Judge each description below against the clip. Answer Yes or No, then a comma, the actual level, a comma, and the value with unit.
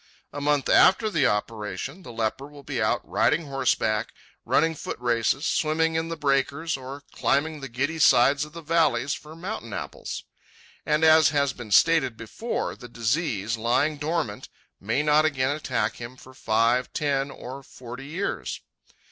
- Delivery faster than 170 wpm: No, average, 160 wpm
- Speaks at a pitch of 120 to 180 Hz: Yes, medium, 140 Hz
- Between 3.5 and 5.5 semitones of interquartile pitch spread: Yes, average, 4.4 semitones